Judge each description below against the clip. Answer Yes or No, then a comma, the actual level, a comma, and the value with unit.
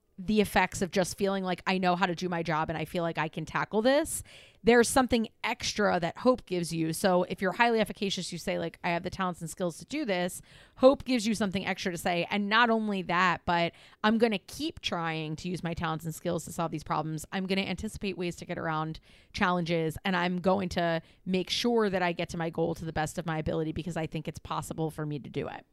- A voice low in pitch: No, medium, 180 Hz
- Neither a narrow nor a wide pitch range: Yes, average, 3.0 semitones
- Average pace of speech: No, fast, 255 wpm